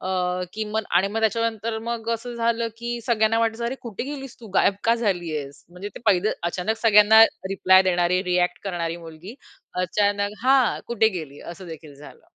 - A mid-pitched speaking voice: No, high, 205 Hz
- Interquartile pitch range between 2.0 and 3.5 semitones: No, average, 4.3 semitones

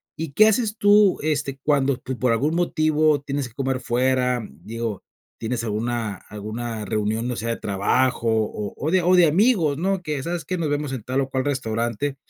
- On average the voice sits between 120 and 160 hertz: Yes, low, 135 Hz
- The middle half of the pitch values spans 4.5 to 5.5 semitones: Yes, average, 5.1 semitones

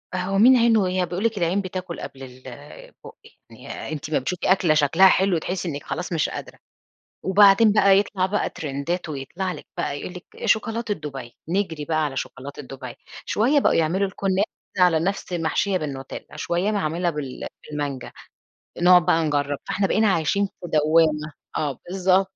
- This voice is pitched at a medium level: Yes, medium, 175 Hz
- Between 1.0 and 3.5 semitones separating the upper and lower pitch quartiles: No, average, 4.5 semitones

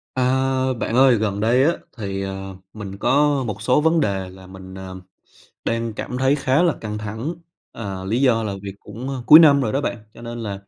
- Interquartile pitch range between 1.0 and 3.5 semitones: No, average, 5.2 semitones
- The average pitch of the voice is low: Yes, low, 115 Hz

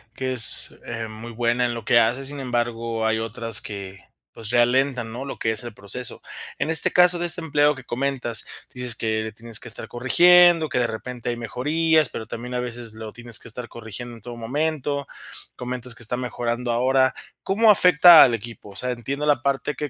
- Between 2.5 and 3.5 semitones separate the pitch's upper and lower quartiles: Yes, average, 3.2 semitones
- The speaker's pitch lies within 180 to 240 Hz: No, low, 120 Hz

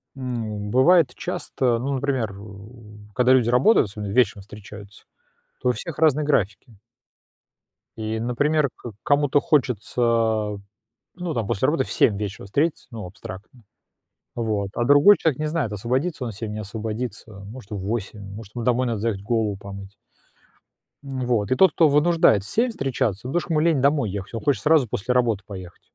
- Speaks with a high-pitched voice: No, low, 120 Hz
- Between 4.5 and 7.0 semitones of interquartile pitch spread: Yes, average, 5.1 semitones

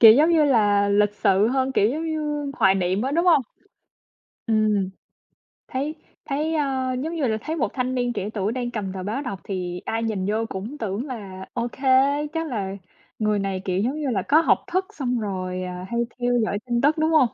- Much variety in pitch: Yes, wide, 5.8 semitones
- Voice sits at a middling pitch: No, high, 235 Hz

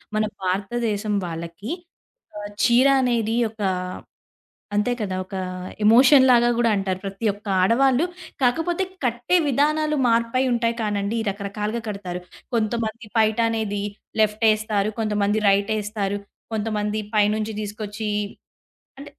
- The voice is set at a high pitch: Yes, high, 215 Hz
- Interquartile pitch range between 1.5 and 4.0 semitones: Yes, narrow, 2.4 semitones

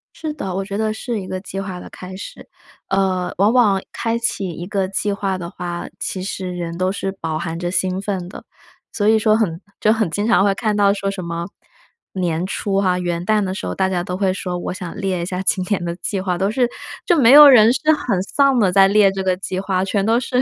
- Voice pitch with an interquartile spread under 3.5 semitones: Yes, narrow, 2.5 semitones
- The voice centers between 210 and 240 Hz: No, high, 195 Hz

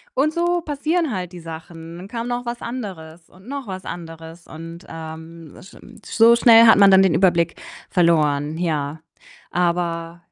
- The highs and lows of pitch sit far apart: Yes, wide, 5.8 semitones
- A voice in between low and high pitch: Yes, medium, 175 Hz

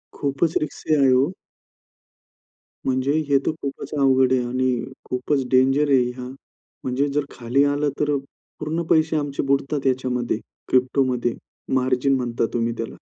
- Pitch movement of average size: No, narrow, 2.0 semitones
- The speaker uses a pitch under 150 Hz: Yes, low, 135 Hz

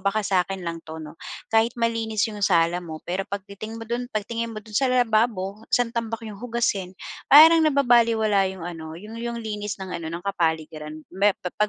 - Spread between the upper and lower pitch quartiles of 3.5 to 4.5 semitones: Yes, average, 4.1 semitones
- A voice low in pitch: No, high, 210 Hz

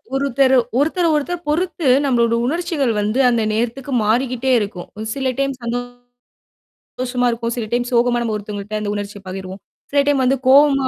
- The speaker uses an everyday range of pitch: Yes, average, 3.9 semitones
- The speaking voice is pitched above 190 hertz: Yes, high, 245 Hz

